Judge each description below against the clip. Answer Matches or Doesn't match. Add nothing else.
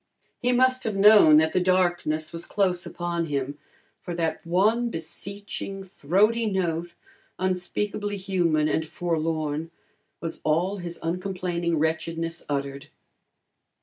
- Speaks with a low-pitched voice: Doesn't match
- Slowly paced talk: Matches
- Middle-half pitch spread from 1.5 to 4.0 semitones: Matches